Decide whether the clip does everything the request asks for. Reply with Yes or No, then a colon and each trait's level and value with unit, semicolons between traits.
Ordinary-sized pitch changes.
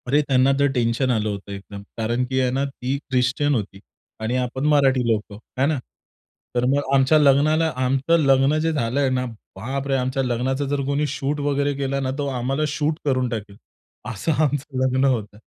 No: narrow, 2.3 semitones